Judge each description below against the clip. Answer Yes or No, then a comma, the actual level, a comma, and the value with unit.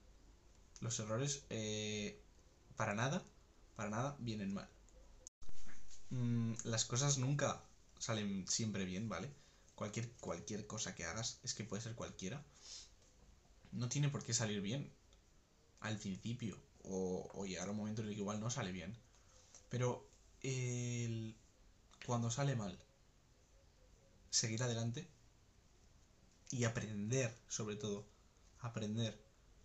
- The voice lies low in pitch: Yes, low, 110 Hz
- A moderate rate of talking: No, slow, 120 wpm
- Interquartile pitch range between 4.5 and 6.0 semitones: No, average, 3.4 semitones